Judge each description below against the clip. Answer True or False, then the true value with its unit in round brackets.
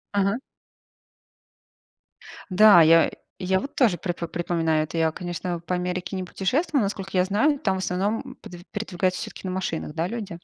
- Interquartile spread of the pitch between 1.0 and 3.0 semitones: True (2.6 semitones)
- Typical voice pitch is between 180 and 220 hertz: True (185 Hz)